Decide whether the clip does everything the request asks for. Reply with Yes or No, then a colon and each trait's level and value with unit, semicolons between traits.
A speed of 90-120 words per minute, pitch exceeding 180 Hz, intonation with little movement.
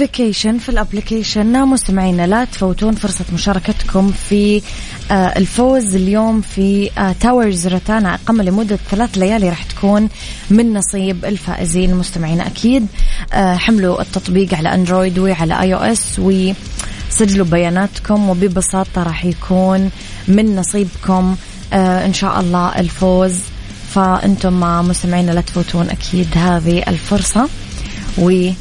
Yes: average, 110 wpm; high, 190 Hz; narrow, 2.3 semitones